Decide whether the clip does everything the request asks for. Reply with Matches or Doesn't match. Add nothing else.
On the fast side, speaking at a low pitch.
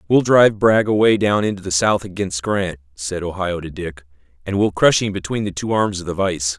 Matches